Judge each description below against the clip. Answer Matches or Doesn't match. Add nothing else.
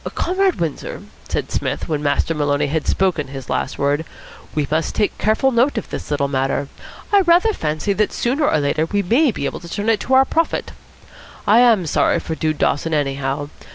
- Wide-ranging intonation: Matches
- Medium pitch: Matches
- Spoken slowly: Doesn't match